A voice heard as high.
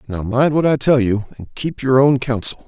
No: low, 125 Hz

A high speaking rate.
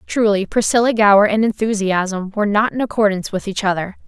No: average, 175 wpm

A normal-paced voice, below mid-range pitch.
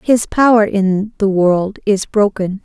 No: average, 160 wpm; high, 205 Hz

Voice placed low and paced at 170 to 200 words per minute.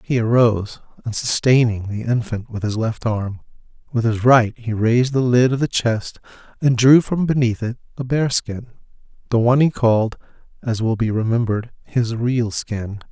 Yes: low, 115 Hz; average, 175 wpm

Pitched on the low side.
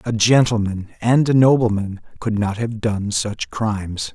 Yes: low, 110 Hz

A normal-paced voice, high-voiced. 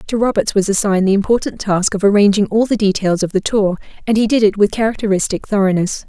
No: fast, 215 wpm; high, 205 Hz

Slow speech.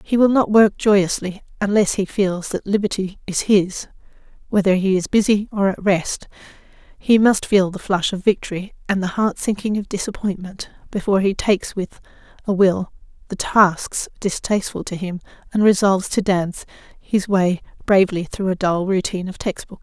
No: average, 170 wpm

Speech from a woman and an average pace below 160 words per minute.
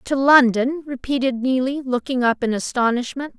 Yes: female; average, 140 wpm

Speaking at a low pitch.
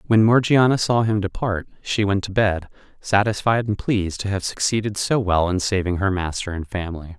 Yes: low, 100 Hz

